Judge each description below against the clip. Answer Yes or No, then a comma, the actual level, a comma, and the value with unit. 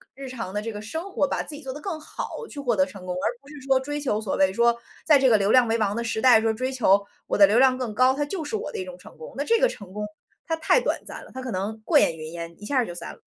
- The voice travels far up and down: Yes, wide, 5.7 semitones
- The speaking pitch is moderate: No, high, 245 Hz